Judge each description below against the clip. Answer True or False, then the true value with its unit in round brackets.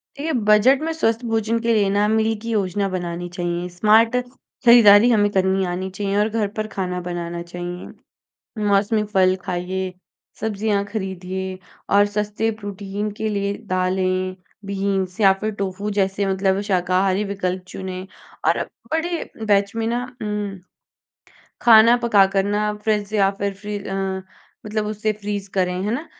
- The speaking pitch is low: False (200 Hz)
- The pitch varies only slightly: True (2.2 semitones)